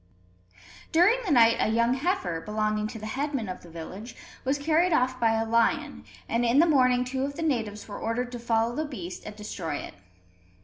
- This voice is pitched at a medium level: No, high, 235 Hz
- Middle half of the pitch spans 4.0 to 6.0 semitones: Yes, average, 4.5 semitones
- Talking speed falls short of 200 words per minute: No, fast, 205 wpm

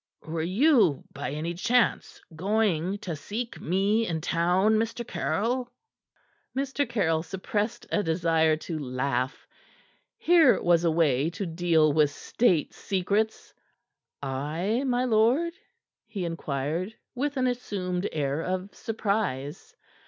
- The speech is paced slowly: Yes, slow, 120 wpm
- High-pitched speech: No, medium, 180 Hz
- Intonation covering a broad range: Yes, wide, 5.7 semitones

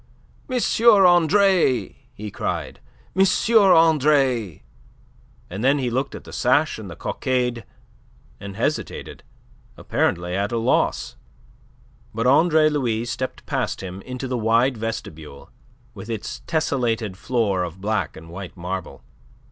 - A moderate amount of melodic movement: No, wide, 5.9 semitones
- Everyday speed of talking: No, slow, 125 wpm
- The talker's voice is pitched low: Yes, low, 115 Hz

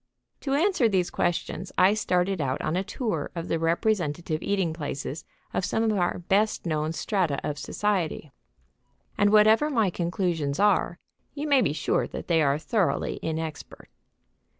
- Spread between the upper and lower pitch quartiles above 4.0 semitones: Yes, average, 4.7 semitones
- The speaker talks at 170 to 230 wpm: No, average, 155 wpm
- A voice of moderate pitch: Yes, medium, 180 Hz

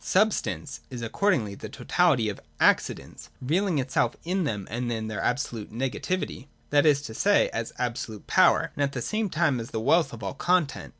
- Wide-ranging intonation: Yes, wide, 6.8 semitones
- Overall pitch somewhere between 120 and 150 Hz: Yes, low, 135 Hz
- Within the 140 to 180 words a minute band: No, average, 200 wpm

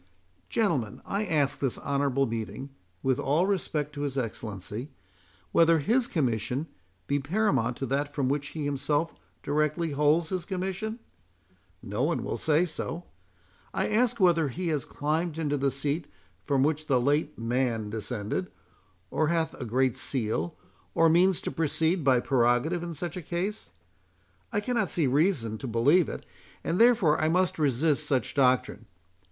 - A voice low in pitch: No, medium, 150 Hz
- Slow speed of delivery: No, average, 155 wpm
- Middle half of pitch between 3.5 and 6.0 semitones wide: Yes, average, 4.5 semitones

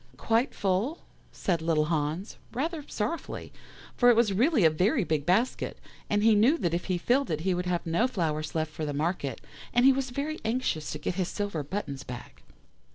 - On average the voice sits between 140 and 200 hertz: Yes, medium, 185 Hz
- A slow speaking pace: No, average, 200 wpm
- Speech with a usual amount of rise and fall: No, wide, 7.4 semitones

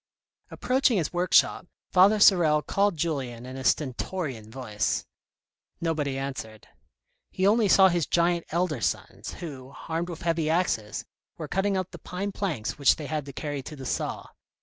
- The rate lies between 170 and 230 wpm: No, average, 160 wpm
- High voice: No, medium, 160 Hz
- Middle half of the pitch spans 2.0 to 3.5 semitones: No, average, 5.3 semitones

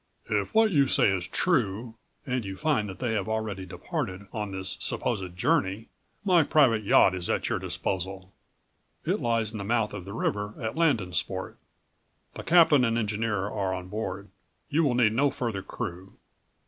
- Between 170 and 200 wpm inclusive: Yes, average, 175 wpm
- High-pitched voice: No, low, 105 Hz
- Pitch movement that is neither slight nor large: Yes, average, 4.2 semitones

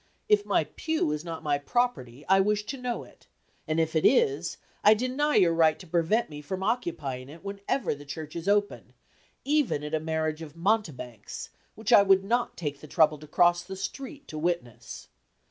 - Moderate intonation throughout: No, wide, 6.4 semitones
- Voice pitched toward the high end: No, medium, 175 Hz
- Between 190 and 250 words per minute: Yes, average, 195 wpm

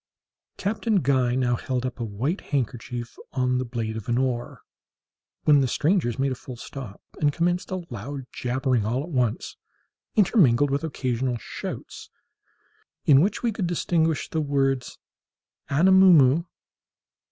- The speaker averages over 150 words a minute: No, average, 145 wpm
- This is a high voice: No, low, 135 Hz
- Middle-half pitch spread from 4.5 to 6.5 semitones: Yes, average, 4.8 semitones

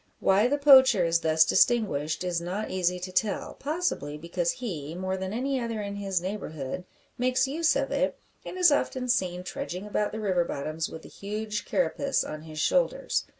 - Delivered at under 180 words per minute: No, average, 190 wpm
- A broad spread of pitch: Yes, wide, 6.6 semitones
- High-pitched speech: Yes, high, 195 Hz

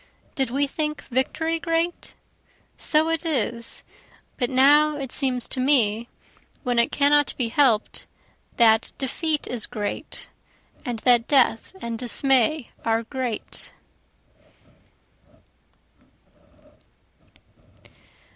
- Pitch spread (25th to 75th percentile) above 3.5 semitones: Yes, average, 3.9 semitones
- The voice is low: No, very high, 260 Hz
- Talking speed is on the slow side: Yes, slow, 100 wpm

